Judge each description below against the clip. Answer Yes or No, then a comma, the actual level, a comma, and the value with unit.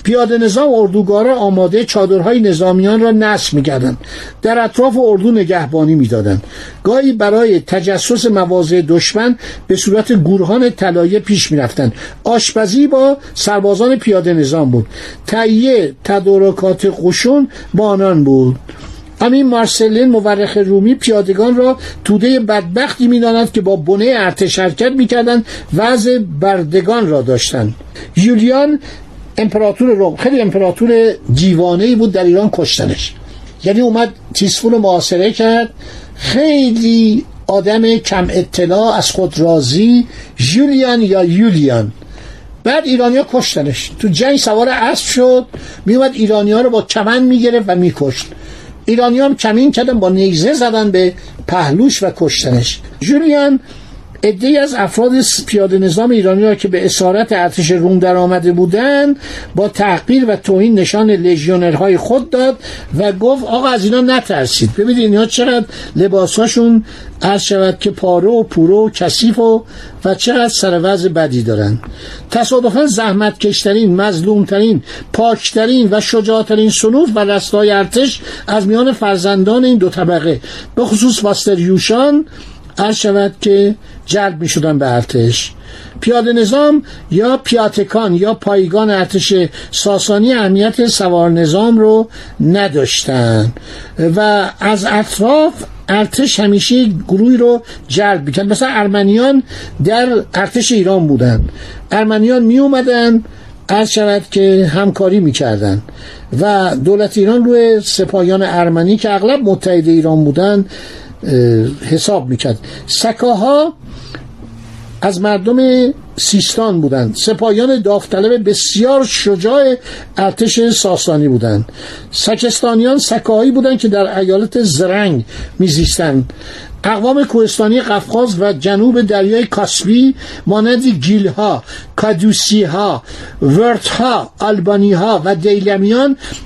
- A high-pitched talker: Yes, high, 205 Hz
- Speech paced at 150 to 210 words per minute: No, average, 120 wpm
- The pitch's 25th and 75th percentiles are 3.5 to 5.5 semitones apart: Yes, average, 4.2 semitones